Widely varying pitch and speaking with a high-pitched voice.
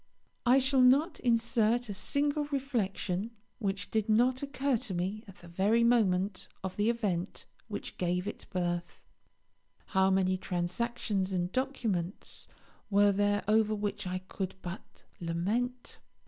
No: average, 4.5 semitones; high, 205 Hz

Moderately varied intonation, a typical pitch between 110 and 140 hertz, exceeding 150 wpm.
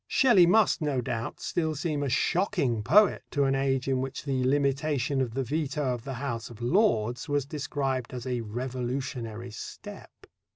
Yes: average, 3.2 semitones; low, 135 Hz; average, 170 wpm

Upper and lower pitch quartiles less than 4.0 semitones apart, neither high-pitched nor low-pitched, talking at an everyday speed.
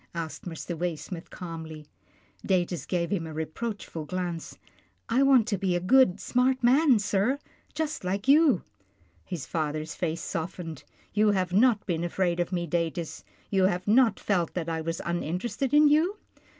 No: wide, 5.5 semitones; medium, 180 Hz; average, 165 wpm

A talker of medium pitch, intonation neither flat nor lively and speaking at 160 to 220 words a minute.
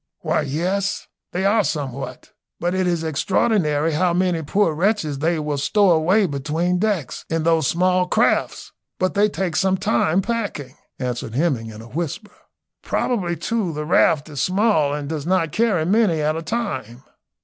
Yes: medium, 165 Hz; average, 4.3 semitones; average, 165 wpm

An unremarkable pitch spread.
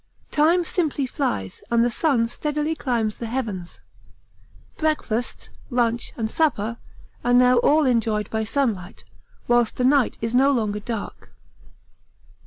Yes: average, 4.2 semitones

